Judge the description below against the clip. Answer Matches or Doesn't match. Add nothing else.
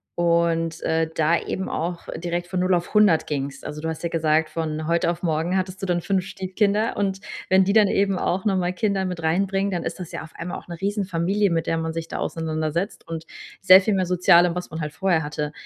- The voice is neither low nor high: Matches